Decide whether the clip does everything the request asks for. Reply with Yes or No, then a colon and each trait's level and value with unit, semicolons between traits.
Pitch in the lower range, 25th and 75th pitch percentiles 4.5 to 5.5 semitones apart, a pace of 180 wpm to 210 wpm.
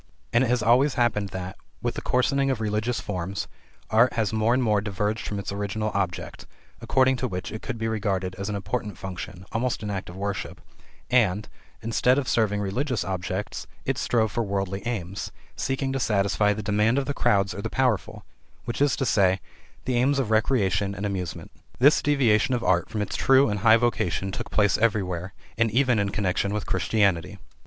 No: low, 105 Hz; average, 3.6 semitones; average, 190 wpm